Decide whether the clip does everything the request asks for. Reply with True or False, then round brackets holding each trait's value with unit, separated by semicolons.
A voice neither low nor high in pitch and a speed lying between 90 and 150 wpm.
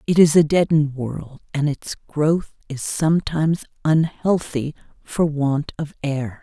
True (150 Hz; 140 wpm)